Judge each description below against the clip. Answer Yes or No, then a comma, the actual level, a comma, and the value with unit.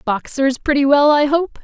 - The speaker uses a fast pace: No, average, 185 wpm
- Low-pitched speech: No, very high, 285 Hz